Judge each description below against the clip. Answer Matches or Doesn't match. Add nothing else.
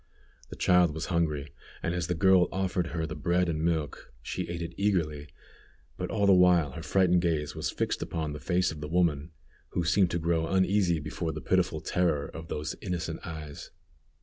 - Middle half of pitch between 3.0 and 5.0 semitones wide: Doesn't match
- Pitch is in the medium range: Doesn't match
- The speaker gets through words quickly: Doesn't match